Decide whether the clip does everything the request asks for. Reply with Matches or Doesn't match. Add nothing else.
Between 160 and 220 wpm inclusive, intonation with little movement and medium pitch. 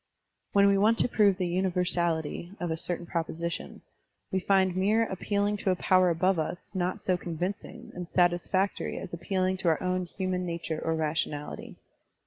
Matches